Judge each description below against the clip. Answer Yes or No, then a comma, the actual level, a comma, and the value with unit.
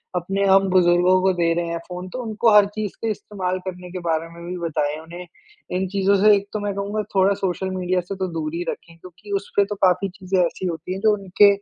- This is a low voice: No, medium, 185 Hz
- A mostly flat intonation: Yes, narrow, 2.3 semitones